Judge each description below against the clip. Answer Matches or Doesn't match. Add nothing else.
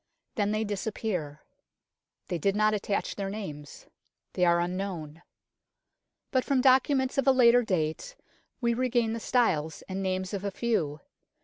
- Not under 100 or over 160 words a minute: Matches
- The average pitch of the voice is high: Matches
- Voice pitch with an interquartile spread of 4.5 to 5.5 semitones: Matches